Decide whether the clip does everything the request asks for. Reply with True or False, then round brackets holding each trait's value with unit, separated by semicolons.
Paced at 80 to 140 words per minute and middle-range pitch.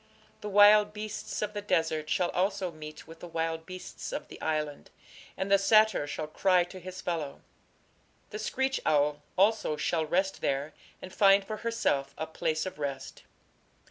False (170 wpm; 180 Hz)